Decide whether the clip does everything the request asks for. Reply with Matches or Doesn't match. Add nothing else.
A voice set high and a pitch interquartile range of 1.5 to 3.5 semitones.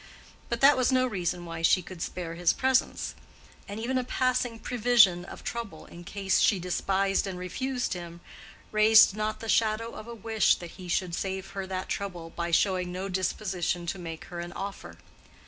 Doesn't match